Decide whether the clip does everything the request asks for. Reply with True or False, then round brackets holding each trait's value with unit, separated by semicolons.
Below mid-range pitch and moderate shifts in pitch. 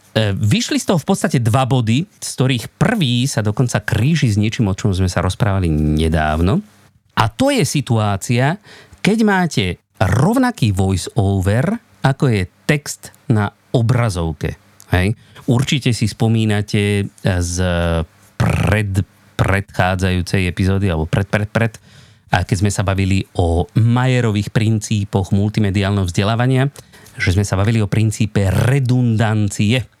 True (110 Hz; 4.3 semitones)